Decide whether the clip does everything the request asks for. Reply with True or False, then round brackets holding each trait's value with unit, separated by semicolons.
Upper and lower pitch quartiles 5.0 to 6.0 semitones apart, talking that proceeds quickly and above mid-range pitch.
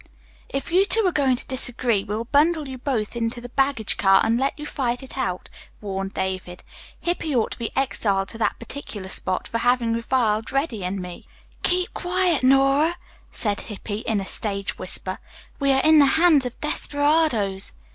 False (5.5 semitones; 180 wpm; 245 Hz)